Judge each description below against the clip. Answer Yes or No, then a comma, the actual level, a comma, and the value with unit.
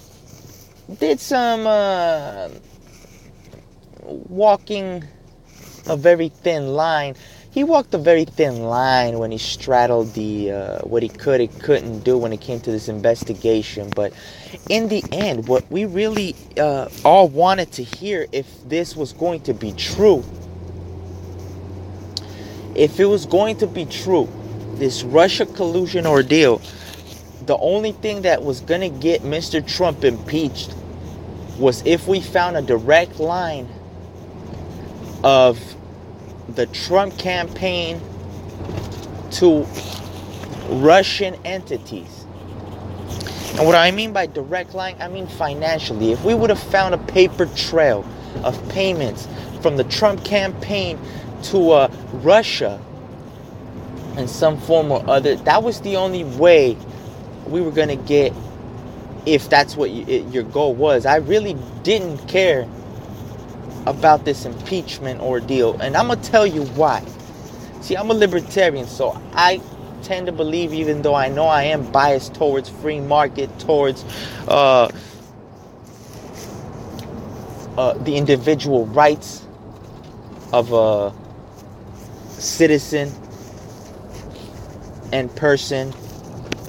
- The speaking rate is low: Yes, slow, 125 wpm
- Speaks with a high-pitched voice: No, low, 130 Hz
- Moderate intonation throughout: No, wide, 7.6 semitones